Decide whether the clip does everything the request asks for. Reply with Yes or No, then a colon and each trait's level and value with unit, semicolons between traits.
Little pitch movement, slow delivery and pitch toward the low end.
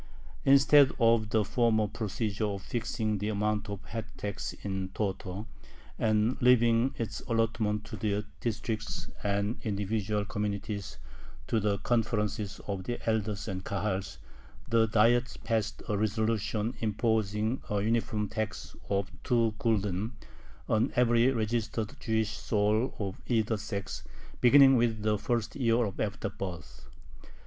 Yes: narrow, 2.0 semitones; slow, 130 wpm; low, 110 Hz